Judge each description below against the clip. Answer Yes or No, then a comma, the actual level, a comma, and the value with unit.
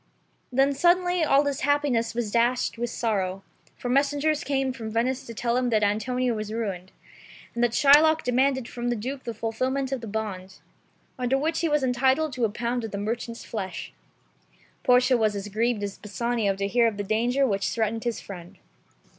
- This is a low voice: No, high, 240 Hz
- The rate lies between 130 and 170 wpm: No, average, 190 wpm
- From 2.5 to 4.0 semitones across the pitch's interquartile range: Yes, average, 3.6 semitones